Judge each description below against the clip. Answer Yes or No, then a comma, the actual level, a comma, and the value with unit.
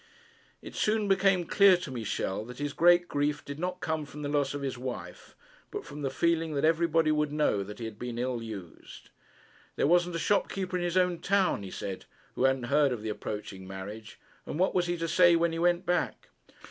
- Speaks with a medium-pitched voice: Yes, medium, 150 Hz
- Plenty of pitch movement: Yes, wide, 6.0 semitones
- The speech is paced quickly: Yes, fast, 215 wpm